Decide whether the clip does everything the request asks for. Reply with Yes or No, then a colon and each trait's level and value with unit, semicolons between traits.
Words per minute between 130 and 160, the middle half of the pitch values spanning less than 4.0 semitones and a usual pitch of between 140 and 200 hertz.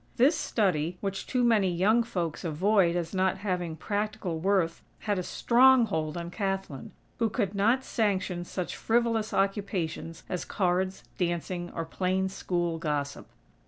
Yes: average, 145 wpm; average, 3.5 semitones; high, 190 Hz